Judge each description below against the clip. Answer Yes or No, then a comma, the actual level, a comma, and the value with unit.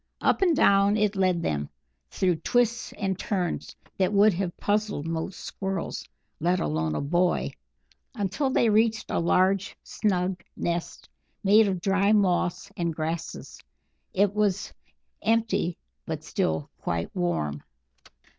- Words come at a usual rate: No, slow, 130 wpm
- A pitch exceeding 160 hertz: Yes, high, 190 Hz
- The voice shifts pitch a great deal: No, average, 3.3 semitones